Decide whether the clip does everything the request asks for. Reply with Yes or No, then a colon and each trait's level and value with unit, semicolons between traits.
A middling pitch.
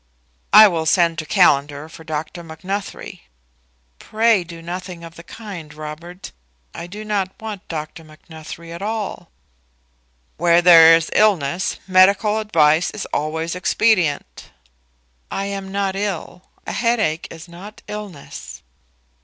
Yes: medium, 175 Hz